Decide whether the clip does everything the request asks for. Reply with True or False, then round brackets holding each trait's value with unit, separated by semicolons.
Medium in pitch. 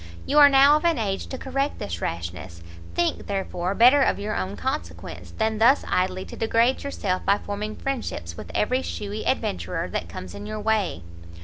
False (205 Hz)